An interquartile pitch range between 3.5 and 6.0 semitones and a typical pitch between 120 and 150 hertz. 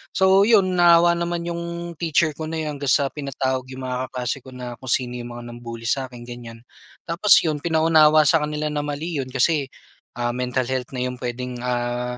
Yes: average, 4.7 semitones; low, 135 Hz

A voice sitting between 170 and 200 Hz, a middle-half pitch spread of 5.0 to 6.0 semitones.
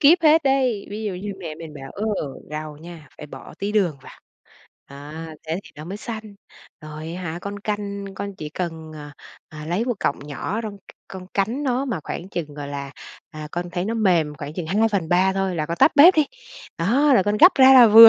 Yes: medium, 185 Hz; wide, 5.6 semitones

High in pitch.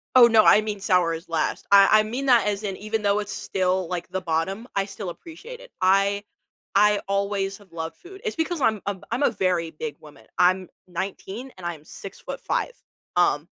Yes: high, 195 Hz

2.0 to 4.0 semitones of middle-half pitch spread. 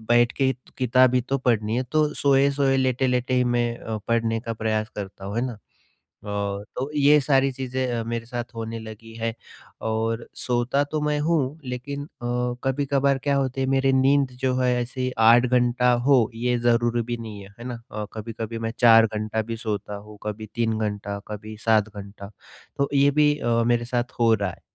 Yes: average, 2.9 semitones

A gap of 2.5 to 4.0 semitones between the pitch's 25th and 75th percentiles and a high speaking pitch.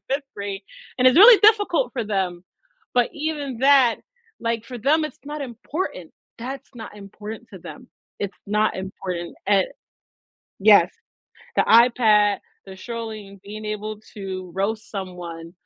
No: average, 4.6 semitones; high, 215 Hz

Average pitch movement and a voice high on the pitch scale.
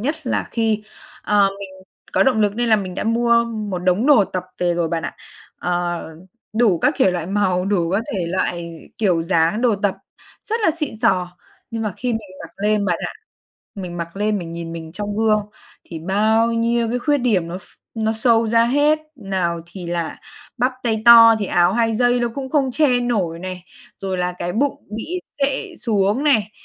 Yes: average, 4.6 semitones; high, 210 Hz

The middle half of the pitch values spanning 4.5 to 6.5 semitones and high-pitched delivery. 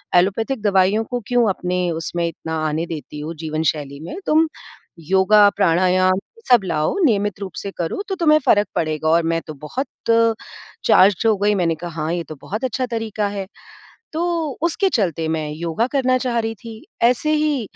Yes: wide, 5.6 semitones; high, 195 Hz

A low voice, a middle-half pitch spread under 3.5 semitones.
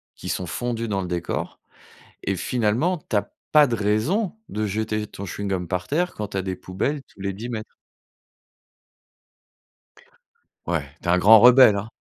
No: low, 105 Hz; average, 4.0 semitones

